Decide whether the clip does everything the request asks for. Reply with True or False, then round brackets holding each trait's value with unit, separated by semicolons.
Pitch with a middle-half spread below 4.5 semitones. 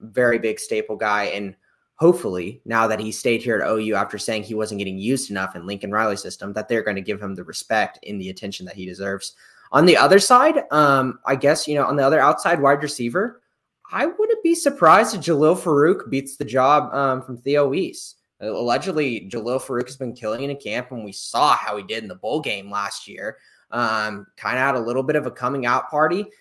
False (5.5 semitones)